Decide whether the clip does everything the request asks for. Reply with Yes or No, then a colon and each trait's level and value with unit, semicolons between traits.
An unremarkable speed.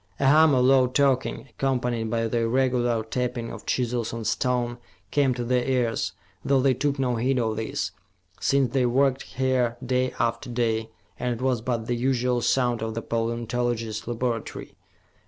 Yes: average, 170 wpm